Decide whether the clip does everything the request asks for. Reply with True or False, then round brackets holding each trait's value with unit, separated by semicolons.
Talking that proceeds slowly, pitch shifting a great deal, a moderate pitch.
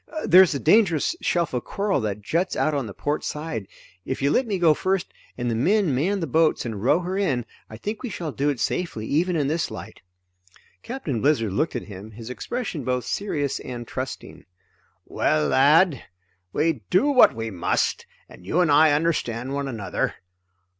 False (190 wpm; 6.8 semitones; 145 Hz)